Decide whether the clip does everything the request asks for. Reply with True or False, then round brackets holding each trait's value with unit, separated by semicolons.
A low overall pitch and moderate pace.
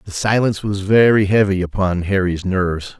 True (95 Hz; 160 wpm)